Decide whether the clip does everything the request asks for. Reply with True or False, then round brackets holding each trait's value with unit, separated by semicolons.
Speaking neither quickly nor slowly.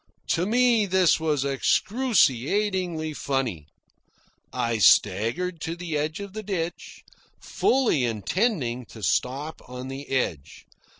False (115 wpm)